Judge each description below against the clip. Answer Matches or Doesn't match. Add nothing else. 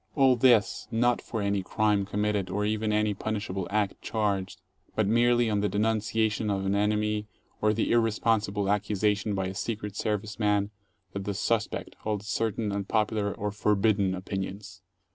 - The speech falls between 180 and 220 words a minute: Doesn't match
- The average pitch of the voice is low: Matches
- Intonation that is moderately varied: Doesn't match